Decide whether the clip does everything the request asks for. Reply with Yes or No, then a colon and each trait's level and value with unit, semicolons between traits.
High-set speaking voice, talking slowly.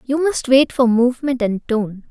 No: very high, 250 Hz; average, 200 wpm